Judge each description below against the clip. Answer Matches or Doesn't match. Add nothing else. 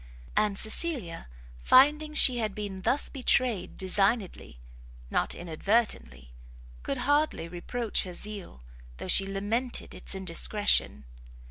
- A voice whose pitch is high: Matches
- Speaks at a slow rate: Matches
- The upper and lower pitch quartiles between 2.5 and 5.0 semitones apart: Doesn't match